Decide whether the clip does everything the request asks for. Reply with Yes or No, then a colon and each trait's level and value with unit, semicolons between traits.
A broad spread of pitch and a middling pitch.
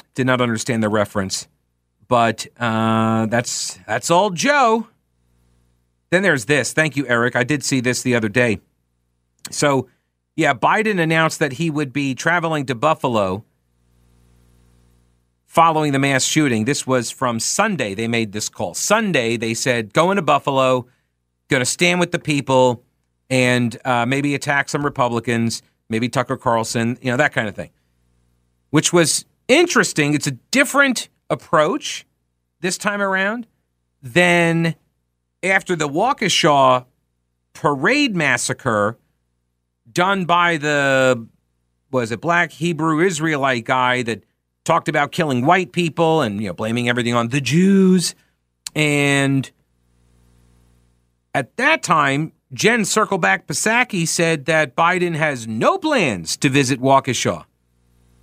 No: wide, 8.4 semitones; low, 130 Hz